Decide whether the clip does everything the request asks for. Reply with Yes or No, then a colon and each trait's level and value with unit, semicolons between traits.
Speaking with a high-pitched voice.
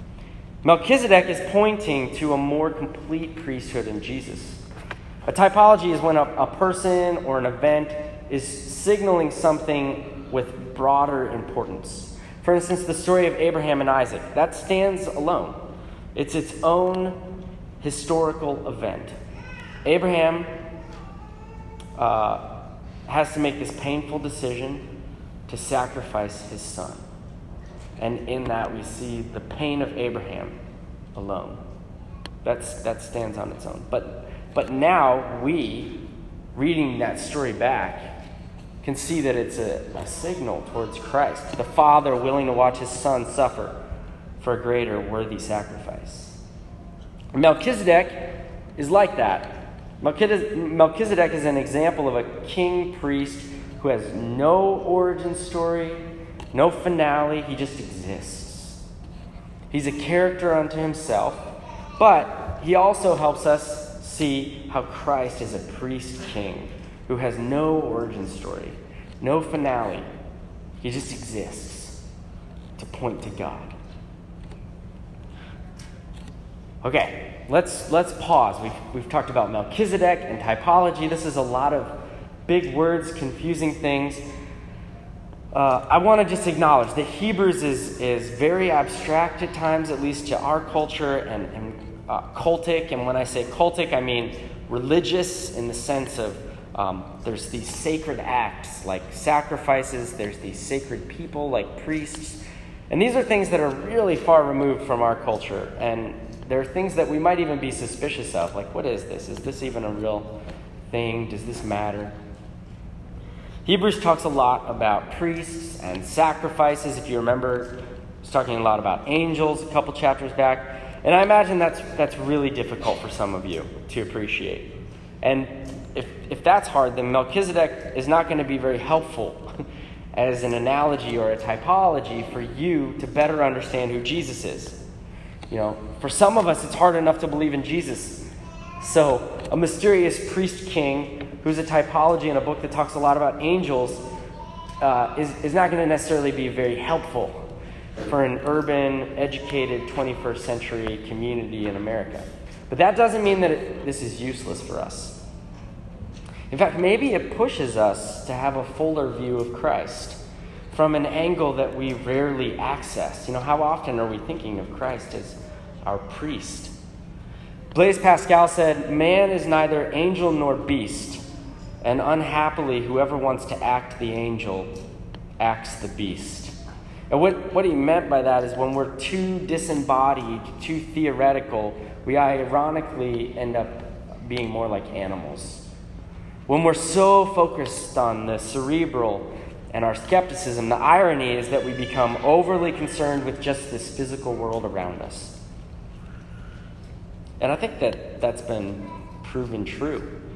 No: low, 135 Hz